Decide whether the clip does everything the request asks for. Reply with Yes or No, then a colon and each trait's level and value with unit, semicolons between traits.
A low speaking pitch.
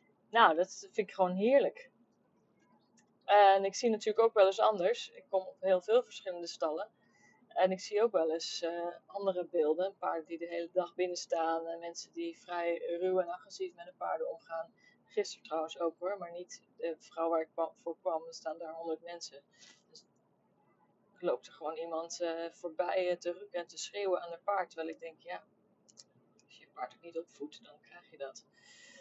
No: medium, 175 Hz